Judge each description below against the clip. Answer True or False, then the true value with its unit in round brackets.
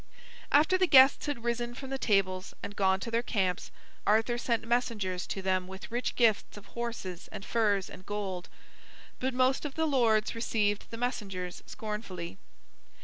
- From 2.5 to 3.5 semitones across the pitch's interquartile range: False (4.1 semitones)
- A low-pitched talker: False (220 Hz)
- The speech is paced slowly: False (165 wpm)